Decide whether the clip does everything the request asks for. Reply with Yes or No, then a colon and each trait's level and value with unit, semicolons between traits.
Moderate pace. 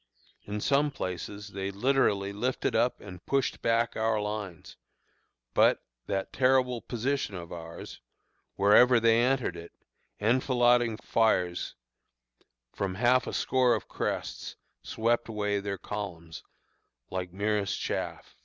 No: slow, 120 wpm